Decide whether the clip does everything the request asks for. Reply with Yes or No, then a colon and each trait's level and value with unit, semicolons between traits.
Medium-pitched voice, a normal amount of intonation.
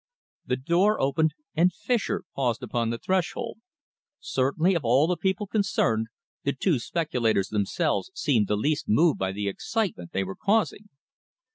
No: medium, 145 Hz; wide, 8.4 semitones